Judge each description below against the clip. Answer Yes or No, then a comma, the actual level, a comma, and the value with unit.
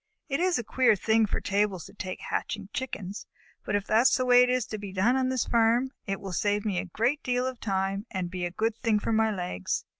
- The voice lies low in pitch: No, high, 215 Hz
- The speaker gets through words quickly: Yes, fast, 260 wpm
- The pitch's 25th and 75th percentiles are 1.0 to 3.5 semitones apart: No, average, 4.1 semitones